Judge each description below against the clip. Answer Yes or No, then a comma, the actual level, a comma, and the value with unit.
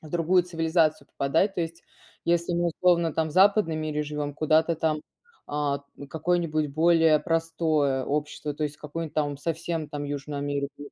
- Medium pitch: Yes, medium, 155 Hz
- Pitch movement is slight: Yes, narrow, 2.2 semitones